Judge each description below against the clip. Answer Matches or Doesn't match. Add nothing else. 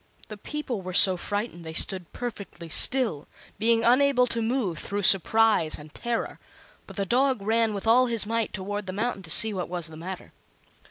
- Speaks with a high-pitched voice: Matches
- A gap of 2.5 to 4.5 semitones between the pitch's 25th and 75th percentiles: Matches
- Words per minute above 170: Matches